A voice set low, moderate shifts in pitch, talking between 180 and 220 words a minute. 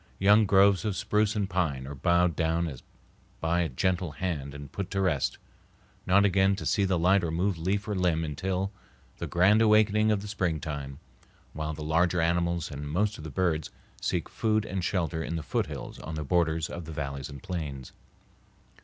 Yes: very low, 85 Hz; average, 3.9 semitones; average, 190 wpm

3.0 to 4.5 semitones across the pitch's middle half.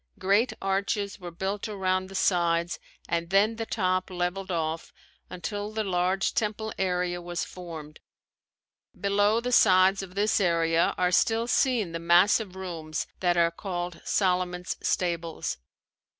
No: narrow, 2.6 semitones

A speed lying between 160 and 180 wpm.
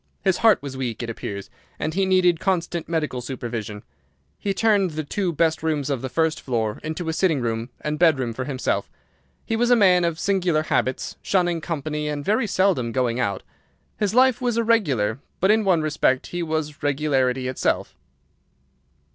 Yes: average, 175 wpm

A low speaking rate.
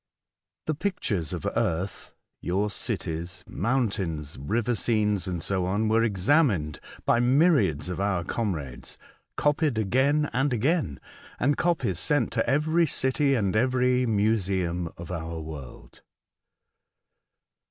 Yes: slow, 130 wpm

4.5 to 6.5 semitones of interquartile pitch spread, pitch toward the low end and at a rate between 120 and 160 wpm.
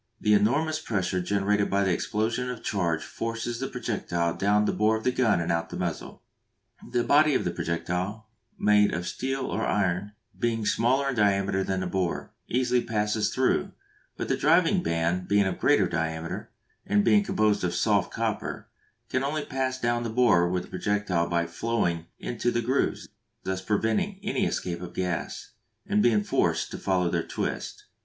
No: average, 4.8 semitones; low, 105 Hz; average, 180 wpm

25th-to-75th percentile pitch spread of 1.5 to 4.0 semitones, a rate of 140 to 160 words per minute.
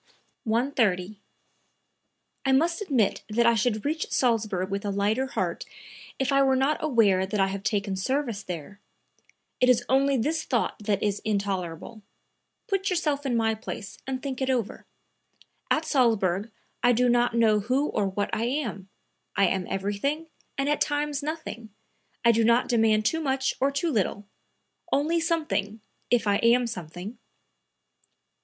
No: average, 5.1 semitones; average, 155 wpm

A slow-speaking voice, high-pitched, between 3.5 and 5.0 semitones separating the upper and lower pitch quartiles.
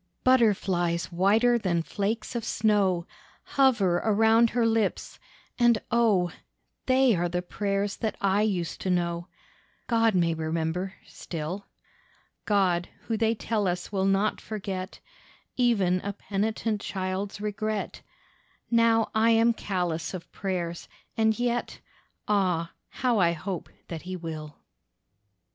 Yes: slow, 125 wpm; high, 200 Hz; average, 3.9 semitones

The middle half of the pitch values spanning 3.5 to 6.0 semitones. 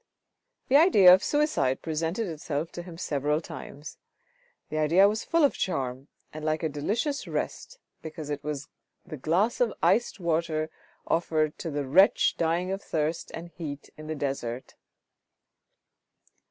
Yes: average, 3.9 semitones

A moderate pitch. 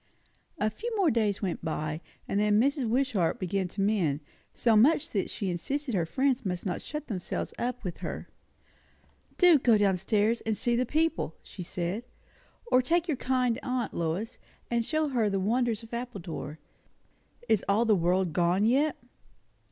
No: high, 220 Hz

